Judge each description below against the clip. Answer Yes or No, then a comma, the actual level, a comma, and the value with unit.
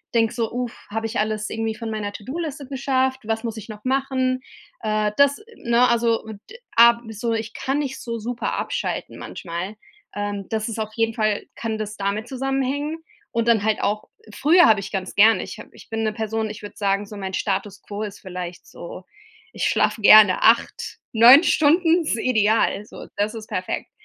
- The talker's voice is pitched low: No, high, 225 Hz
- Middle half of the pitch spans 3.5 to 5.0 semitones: No, average, 3.1 semitones